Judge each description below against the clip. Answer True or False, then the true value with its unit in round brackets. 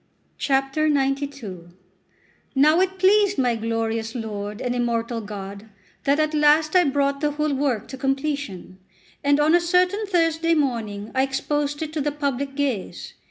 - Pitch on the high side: True (280 Hz)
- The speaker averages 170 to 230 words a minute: False (150 wpm)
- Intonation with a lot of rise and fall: False (4.8 semitones)